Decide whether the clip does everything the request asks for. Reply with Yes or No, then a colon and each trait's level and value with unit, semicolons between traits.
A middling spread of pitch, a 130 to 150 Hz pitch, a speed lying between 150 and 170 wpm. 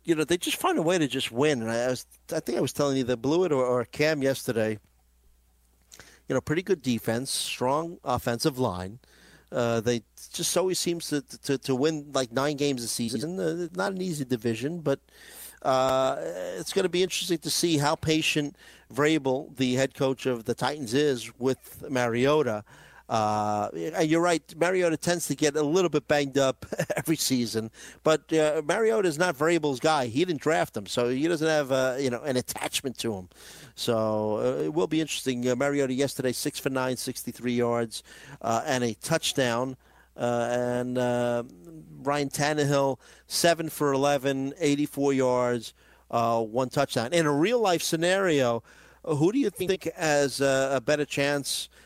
No: average, 4.2 semitones; low, 135 Hz; average, 180 wpm